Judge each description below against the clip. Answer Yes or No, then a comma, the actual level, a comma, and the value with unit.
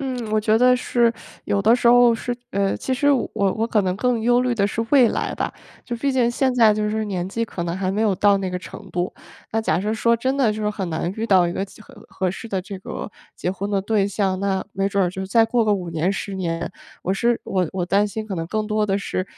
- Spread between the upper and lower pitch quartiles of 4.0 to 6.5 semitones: No, average, 3.3 semitones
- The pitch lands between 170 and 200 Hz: No, high, 210 Hz